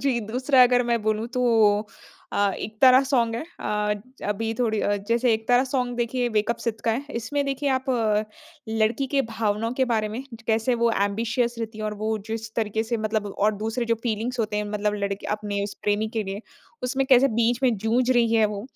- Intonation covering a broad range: No, narrow, 2.6 semitones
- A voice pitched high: Yes, high, 225 Hz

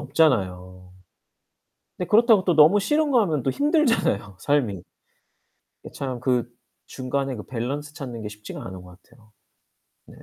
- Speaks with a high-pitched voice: No, low, 135 Hz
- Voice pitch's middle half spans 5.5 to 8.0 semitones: No, wide, 8.6 semitones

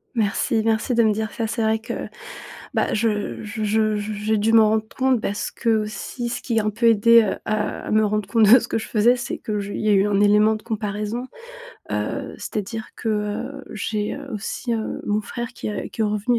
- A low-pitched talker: No, high, 215 Hz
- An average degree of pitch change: No, narrow, 1.6 semitones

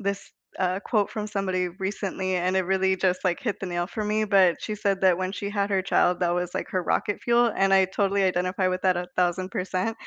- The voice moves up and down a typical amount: No, narrow, 1.6 semitones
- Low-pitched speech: No, high, 190 Hz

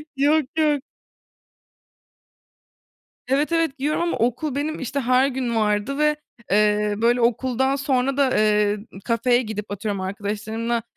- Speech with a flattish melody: No, average, 4.6 semitones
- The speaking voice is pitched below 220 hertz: No, high, 245 Hz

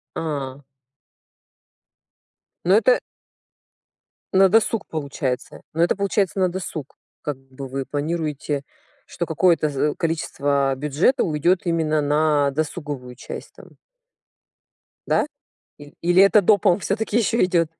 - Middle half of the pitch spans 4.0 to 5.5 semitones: Yes, average, 4.5 semitones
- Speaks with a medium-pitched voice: Yes, medium, 155 Hz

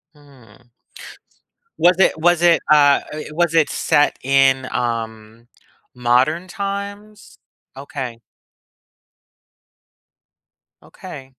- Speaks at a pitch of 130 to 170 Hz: Yes, medium, 140 Hz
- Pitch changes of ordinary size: No, wide, 5.9 semitones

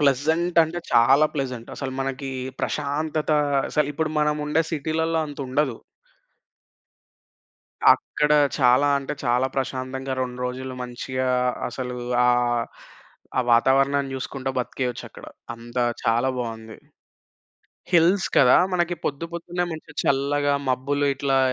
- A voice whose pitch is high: No, low, 135 Hz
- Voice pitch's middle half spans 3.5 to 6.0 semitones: No, average, 2.9 semitones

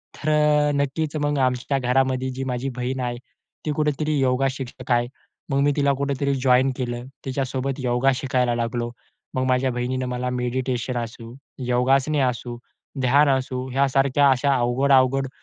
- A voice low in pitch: Yes, low, 130 Hz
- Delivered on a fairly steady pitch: Yes, narrow, 1.8 semitones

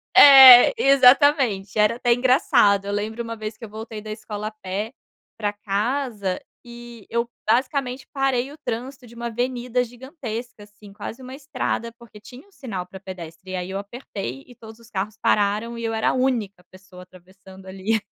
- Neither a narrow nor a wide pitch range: Yes, average, 3.7 semitones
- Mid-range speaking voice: No, high, 225 Hz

